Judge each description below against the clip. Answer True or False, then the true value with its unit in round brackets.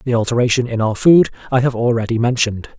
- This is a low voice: True (120 Hz)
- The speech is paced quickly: False (195 wpm)